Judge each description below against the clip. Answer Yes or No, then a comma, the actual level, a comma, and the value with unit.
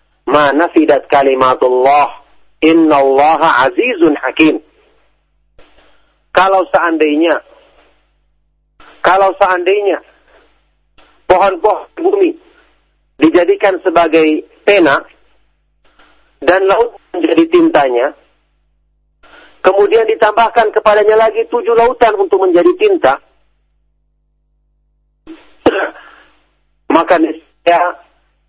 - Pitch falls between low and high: Yes, medium, 175 Hz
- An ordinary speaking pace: No, slow, 60 wpm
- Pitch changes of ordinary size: No, wide, 7.4 semitones